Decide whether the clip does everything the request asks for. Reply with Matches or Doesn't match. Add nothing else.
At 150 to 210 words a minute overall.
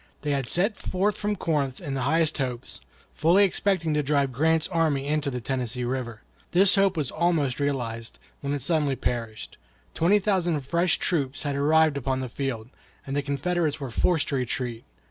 Matches